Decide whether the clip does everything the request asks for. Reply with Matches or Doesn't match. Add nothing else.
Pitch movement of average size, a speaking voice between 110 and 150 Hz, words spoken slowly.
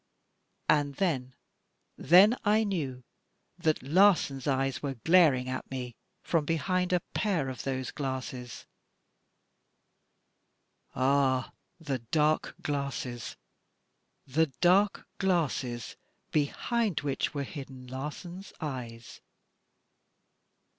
Matches